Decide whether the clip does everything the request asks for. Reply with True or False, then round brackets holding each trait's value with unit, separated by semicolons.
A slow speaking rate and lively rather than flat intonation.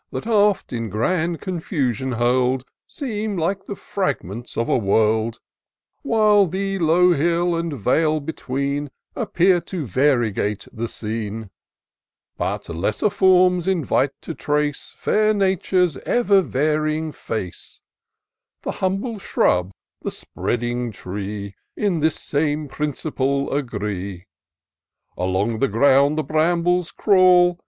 True (115 wpm; 7.4 semitones)